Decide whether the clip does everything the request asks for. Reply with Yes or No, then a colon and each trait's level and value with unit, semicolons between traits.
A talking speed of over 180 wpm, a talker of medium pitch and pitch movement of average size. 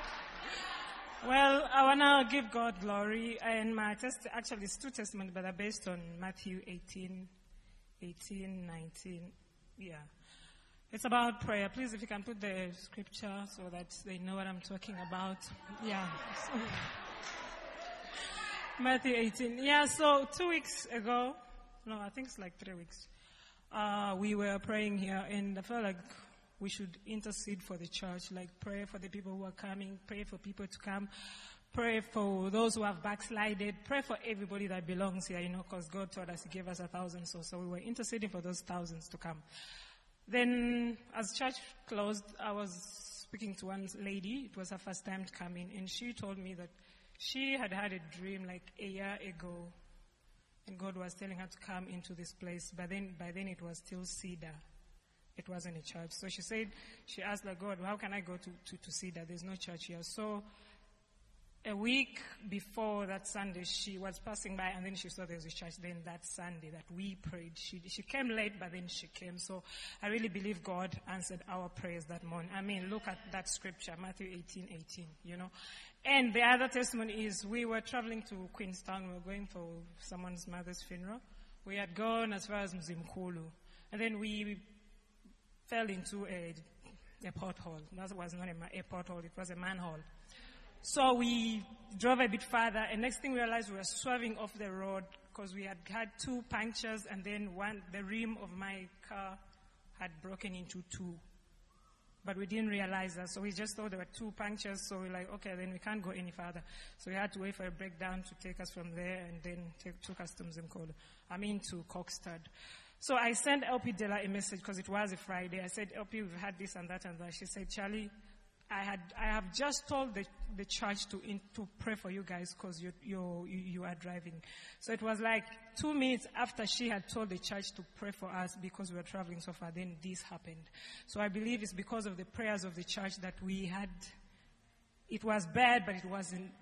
No: average, 200 wpm; high, 195 Hz; average, 3.0 semitones